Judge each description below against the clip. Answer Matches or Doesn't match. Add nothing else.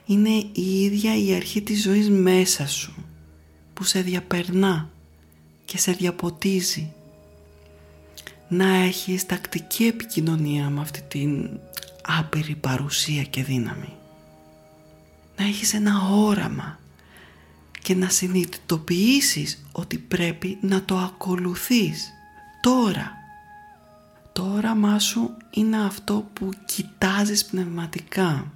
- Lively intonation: Matches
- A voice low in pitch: Doesn't match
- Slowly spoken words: Matches